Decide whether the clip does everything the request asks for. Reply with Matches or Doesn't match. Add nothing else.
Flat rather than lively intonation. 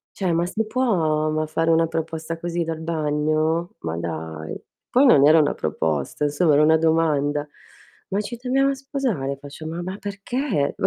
Doesn't match